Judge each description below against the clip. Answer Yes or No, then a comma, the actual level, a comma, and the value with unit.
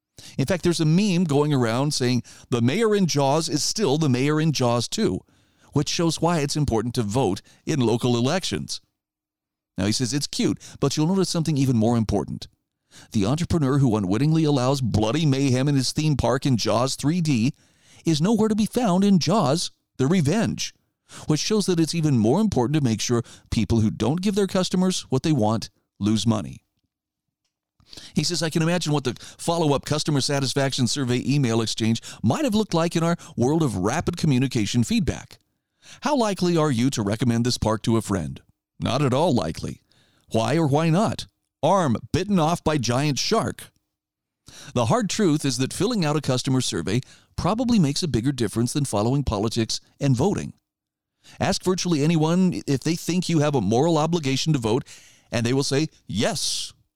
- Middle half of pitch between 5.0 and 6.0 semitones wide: Yes, wide, 5.6 semitones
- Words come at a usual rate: Yes, average, 180 wpm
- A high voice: No, medium, 140 Hz